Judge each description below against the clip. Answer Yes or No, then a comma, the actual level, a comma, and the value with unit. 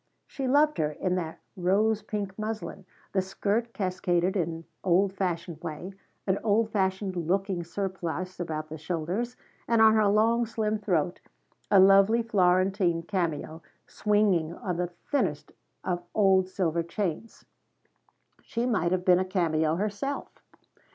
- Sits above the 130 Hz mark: Yes, high, 190 Hz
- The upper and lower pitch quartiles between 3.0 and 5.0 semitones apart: Yes, average, 3.5 semitones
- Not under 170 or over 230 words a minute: No, slow, 135 wpm